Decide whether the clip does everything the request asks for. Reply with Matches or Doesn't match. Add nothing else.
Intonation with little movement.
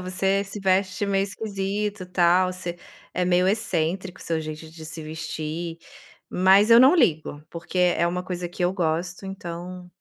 Matches